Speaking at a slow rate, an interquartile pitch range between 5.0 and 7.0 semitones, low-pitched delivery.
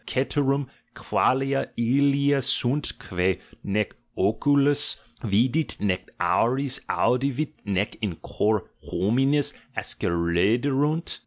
Yes: slow, 85 wpm; average, 5.3 semitones; low, 130 Hz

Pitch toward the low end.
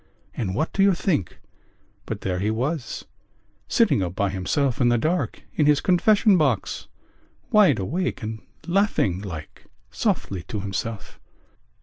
Yes: low, 120 Hz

